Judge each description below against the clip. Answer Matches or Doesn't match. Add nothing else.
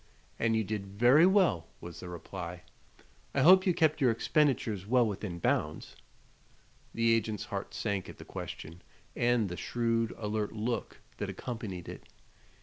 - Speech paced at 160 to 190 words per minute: Doesn't match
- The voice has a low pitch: Matches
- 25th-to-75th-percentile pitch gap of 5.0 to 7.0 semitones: Doesn't match